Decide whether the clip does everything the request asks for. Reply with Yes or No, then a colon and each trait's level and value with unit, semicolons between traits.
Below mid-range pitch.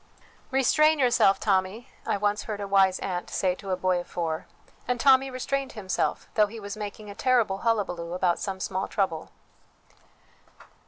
No: high, 200 Hz